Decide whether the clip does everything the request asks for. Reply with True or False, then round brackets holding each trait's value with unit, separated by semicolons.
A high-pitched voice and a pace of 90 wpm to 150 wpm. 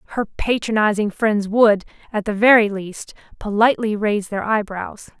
True (210 Hz; 140 wpm)